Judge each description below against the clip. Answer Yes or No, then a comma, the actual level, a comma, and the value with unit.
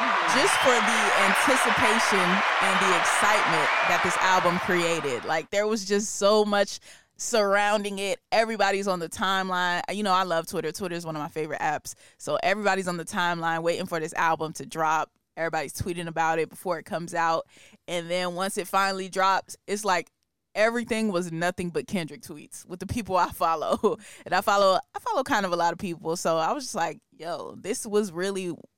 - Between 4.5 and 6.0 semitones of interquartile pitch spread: No, average, 3.4 semitones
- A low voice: No, medium, 180 Hz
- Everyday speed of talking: Yes, average, 195 wpm